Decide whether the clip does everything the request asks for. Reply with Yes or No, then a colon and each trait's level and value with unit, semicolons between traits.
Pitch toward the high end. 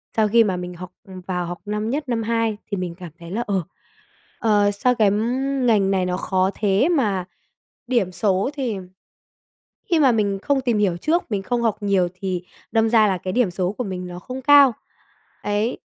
Yes: high, 205 Hz